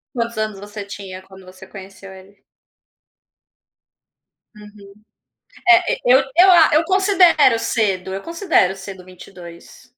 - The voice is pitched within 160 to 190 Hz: No, high, 205 Hz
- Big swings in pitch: Yes, wide, 7.6 semitones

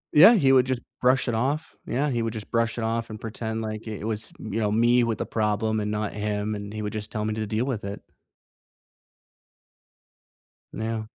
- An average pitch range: No, narrow, 1.8 semitones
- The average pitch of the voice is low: Yes, low, 110 Hz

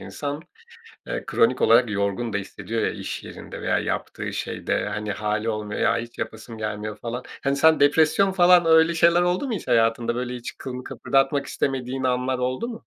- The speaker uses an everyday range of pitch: No, wide, 5.8 semitones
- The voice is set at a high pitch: No, low, 125 Hz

